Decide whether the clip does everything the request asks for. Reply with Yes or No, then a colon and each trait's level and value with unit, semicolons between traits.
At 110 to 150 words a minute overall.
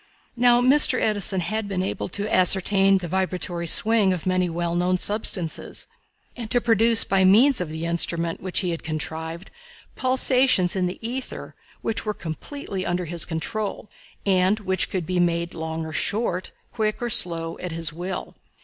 No: average, 165 wpm